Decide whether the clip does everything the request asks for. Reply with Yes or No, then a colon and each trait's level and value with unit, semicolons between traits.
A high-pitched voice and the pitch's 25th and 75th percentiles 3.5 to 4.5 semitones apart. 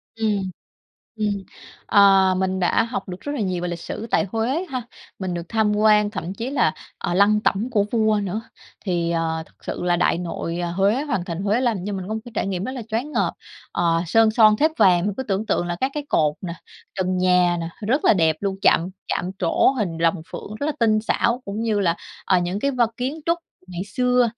Yes: high, 200 Hz; average, 4.1 semitones